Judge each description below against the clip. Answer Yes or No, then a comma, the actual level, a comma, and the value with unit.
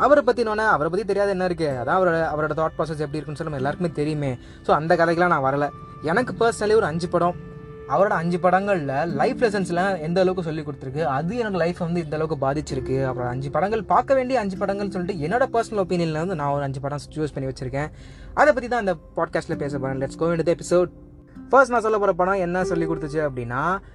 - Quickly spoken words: Yes, fast, 210 wpm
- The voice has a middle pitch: Yes, medium, 170 Hz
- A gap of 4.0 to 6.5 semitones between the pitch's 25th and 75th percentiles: Yes, average, 4.6 semitones